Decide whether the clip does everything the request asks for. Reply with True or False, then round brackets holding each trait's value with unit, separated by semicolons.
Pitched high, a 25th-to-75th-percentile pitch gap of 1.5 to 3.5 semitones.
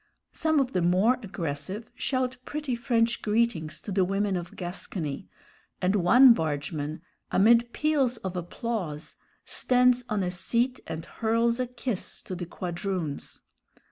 False (205 Hz; 5.5 semitones)